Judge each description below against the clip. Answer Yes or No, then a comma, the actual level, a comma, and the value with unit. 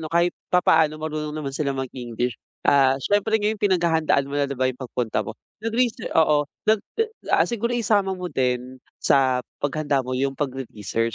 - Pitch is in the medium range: Yes, medium, 145 Hz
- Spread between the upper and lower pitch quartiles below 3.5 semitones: No, wide, 5.4 semitones